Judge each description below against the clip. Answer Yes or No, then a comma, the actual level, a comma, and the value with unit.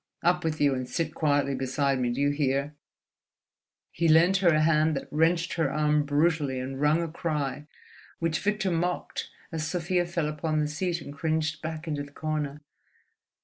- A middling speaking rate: Yes, average, 175 wpm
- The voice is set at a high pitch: No, medium, 155 Hz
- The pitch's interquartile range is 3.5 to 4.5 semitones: No, narrow, 2.5 semitones